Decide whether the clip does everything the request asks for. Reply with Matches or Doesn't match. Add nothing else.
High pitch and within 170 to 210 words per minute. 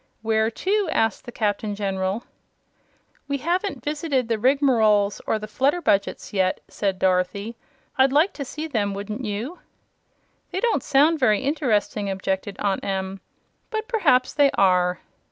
Doesn't match